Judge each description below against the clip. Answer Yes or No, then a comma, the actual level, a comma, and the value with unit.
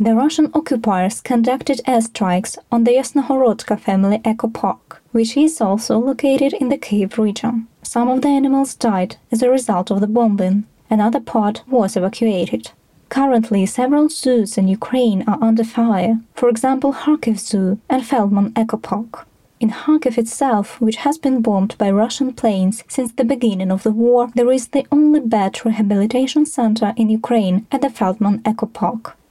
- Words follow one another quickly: Yes, fast, 160 wpm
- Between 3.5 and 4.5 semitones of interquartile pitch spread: Yes, average, 3.9 semitones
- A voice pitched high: Yes, high, 230 Hz